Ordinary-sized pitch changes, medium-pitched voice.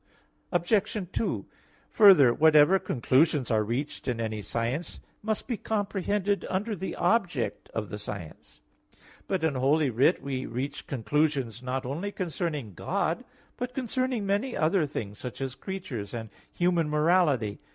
No: wide, 7.5 semitones; medium, 150 Hz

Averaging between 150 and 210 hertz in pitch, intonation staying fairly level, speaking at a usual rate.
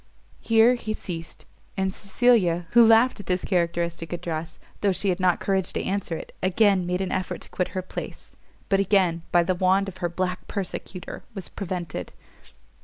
Yes: medium, 185 Hz; narrow, 2.3 semitones; average, 180 wpm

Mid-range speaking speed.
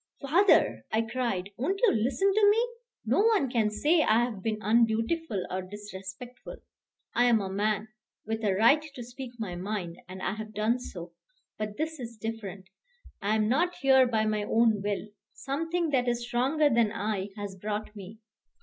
Yes: average, 175 wpm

